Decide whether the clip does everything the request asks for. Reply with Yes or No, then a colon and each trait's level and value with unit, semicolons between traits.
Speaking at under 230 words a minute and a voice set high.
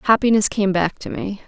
Yes: fast, 205 wpm; high, 200 Hz